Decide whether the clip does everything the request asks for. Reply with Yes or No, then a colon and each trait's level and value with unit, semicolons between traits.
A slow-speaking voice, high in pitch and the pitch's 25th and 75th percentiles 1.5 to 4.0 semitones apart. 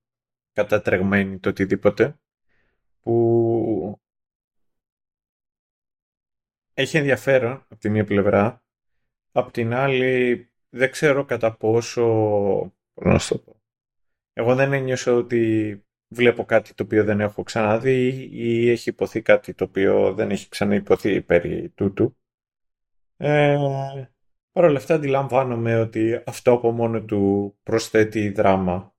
No: slow, 110 wpm; low, 115 Hz; average, 3.0 semitones